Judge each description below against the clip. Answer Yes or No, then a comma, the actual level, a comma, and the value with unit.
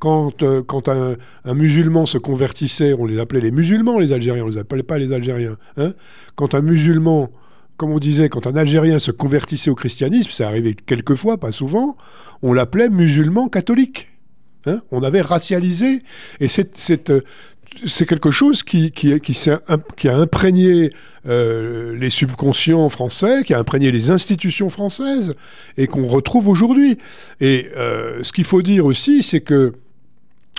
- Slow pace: No, average, 165 wpm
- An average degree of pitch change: No, wide, 5.7 semitones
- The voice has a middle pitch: Yes, medium, 155 Hz